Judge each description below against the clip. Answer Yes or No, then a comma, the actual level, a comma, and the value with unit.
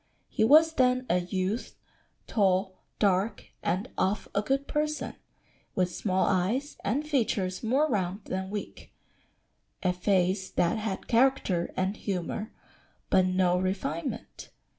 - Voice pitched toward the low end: No, high, 195 Hz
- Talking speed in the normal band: No, slow, 125 wpm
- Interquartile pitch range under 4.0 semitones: No, average, 4.5 semitones